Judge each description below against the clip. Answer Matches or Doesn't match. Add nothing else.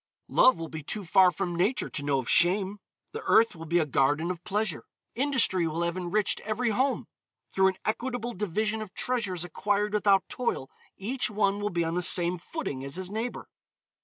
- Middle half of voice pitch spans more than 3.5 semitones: Matches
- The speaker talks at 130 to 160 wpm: Doesn't match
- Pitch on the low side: Doesn't match